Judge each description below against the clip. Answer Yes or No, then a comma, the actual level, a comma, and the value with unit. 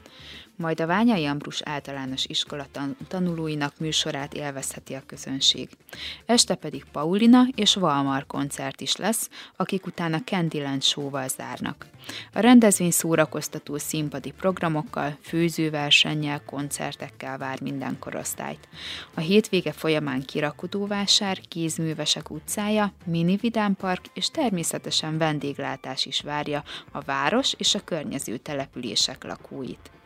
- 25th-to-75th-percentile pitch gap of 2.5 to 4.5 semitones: No, average, 4.9 semitones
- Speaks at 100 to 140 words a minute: Yes, average, 110 wpm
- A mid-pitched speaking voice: Yes, medium, 160 Hz